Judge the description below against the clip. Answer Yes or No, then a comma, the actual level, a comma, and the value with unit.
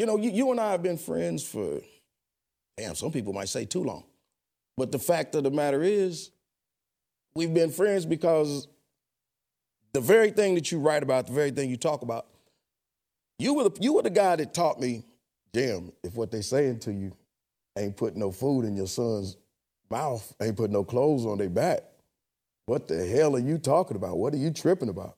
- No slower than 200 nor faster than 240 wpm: Yes, fast, 205 wpm